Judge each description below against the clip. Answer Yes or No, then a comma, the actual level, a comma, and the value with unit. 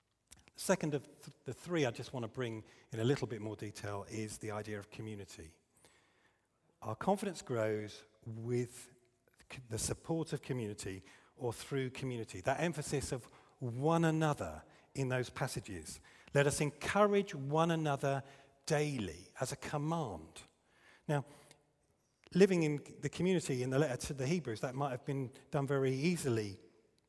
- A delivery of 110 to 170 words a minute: Yes, average, 145 wpm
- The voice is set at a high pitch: No, low, 135 Hz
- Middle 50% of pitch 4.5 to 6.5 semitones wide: Yes, average, 4.9 semitones